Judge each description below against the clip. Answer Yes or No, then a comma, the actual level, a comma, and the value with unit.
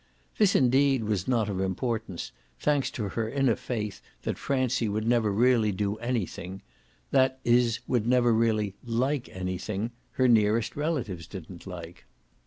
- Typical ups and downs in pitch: Yes, average, 3.9 semitones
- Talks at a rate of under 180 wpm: Yes, average, 145 wpm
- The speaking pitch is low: Yes, low, 115 Hz